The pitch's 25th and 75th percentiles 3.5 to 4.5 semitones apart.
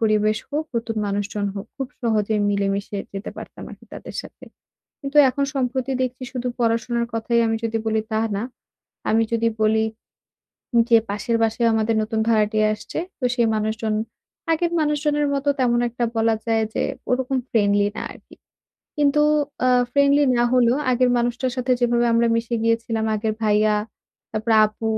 No: narrow, 2.6 semitones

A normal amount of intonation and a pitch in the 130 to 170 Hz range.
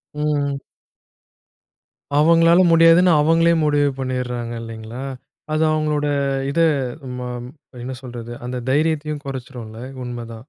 Yes: average, 4.1 semitones; medium, 140 Hz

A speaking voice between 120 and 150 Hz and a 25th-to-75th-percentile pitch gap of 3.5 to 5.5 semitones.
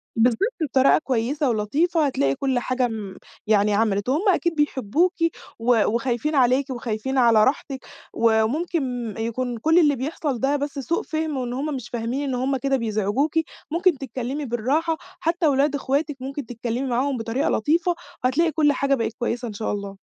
No: very high, 260 Hz; average, 4.1 semitones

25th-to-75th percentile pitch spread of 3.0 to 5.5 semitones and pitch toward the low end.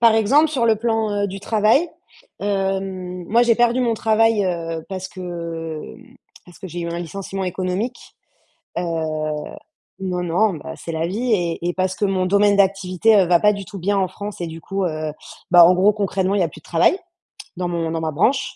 No: average, 3.5 semitones; high, 190 Hz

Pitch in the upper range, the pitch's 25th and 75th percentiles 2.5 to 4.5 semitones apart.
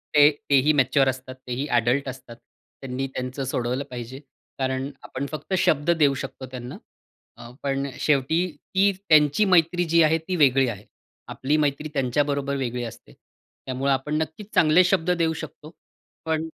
No: medium, 140 Hz; average, 3.2 semitones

